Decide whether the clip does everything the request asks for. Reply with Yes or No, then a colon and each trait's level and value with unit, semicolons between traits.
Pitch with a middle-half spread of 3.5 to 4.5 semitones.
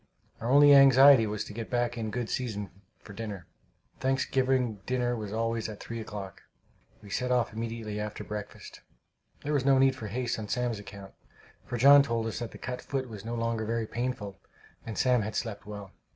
No: average, 3.0 semitones